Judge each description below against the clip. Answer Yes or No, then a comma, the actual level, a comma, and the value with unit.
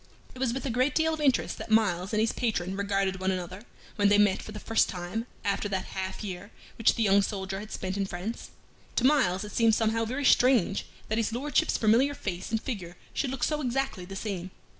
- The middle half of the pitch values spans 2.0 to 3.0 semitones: No, average, 4.2 semitones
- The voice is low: No, high, 210 Hz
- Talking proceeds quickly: Yes, fast, 225 wpm